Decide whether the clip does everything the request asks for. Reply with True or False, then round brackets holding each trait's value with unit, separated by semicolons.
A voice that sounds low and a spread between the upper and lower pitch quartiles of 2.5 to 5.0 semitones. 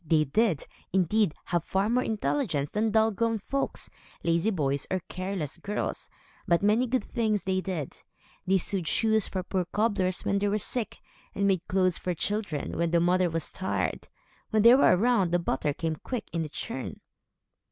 False (190 Hz; 4.3 semitones)